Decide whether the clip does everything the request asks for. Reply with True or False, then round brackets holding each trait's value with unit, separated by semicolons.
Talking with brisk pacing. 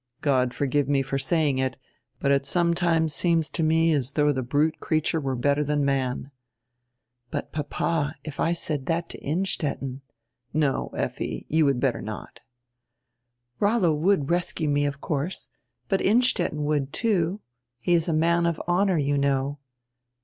False (165 wpm)